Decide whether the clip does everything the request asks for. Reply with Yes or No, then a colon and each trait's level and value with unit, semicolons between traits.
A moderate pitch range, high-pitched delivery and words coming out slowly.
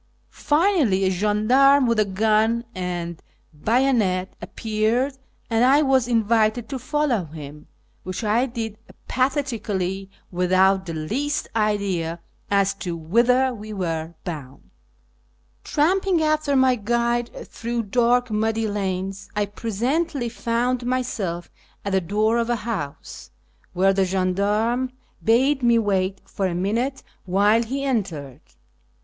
Yes: average, 4.6 semitones; high, 220 Hz; slow, 125 wpm